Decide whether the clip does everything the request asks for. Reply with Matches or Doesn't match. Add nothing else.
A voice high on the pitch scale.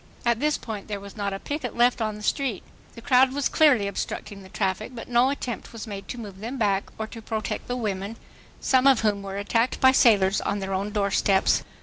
Matches